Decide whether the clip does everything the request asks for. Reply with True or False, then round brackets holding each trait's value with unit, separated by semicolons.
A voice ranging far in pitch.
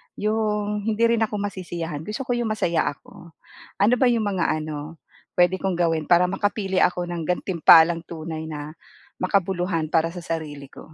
False (4.1 semitones)